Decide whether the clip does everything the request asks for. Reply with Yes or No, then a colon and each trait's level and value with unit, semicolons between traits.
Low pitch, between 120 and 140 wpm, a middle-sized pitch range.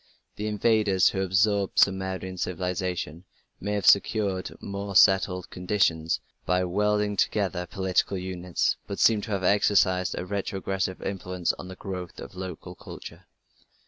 No: very low, 95 Hz; slow, 135 wpm; narrow, 1.7 semitones